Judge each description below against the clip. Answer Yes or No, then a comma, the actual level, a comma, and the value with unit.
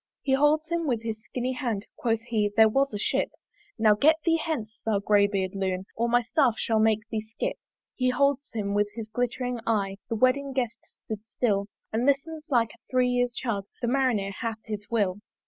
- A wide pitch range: No, average, 3.3 semitones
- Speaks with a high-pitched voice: Yes, high, 230 Hz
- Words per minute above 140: Yes, average, 200 wpm